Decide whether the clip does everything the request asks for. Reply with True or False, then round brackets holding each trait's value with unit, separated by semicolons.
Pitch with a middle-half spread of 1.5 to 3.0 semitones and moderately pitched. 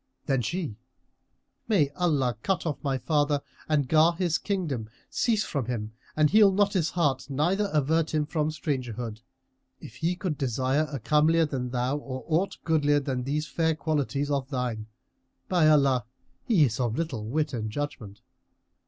False (3.9 semitones; 145 Hz)